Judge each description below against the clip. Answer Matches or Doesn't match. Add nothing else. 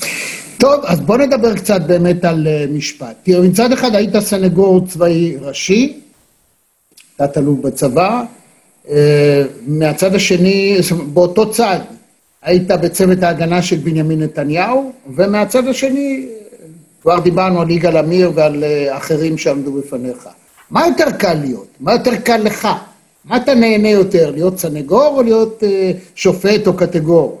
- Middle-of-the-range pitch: Matches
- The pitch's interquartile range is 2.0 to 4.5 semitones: Doesn't match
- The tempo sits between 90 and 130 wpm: Matches